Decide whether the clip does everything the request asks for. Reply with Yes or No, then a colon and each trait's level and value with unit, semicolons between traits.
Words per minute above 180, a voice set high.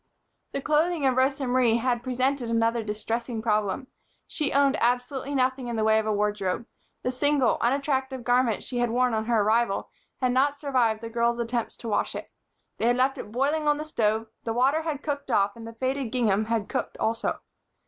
Yes: average, 200 wpm; high, 245 Hz